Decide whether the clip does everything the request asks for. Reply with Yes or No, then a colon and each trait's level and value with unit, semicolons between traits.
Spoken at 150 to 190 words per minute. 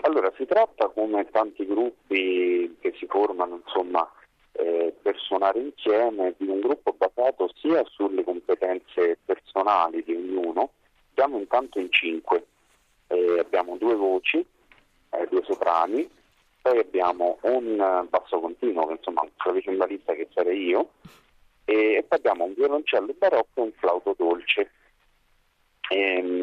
No: average, 135 wpm